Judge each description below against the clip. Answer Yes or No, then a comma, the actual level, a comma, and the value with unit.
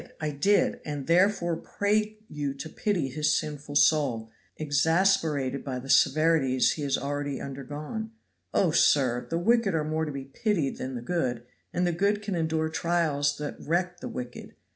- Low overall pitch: No, medium, 155 Hz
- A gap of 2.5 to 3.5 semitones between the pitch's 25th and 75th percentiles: No, average, 3.9 semitones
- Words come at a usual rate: Yes, average, 165 wpm